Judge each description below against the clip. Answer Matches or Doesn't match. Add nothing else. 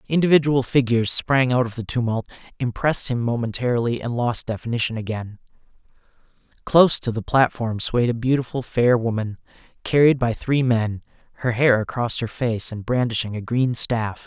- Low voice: Matches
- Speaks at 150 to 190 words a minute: Matches